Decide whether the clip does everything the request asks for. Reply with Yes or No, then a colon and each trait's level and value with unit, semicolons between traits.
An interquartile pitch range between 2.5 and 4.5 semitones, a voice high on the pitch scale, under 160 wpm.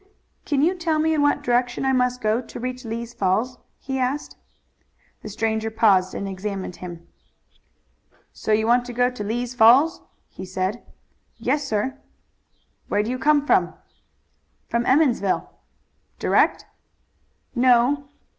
Yes: average, 3.7 semitones; high, 245 Hz; average, 140 wpm